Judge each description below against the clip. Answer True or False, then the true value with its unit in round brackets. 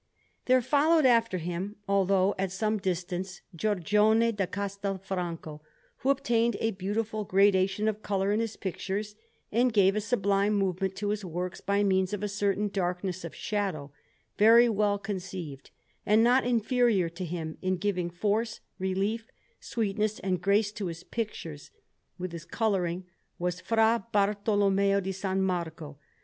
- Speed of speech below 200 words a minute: True (145 wpm)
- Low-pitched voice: False (200 Hz)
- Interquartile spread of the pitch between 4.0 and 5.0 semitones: False (2.6 semitones)